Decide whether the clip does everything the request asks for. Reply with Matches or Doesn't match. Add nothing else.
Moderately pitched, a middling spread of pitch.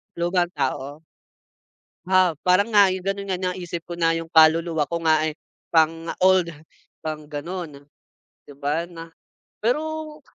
Matches